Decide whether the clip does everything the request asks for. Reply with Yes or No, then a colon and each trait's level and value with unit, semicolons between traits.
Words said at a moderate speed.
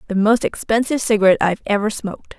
Yes: average, 175 wpm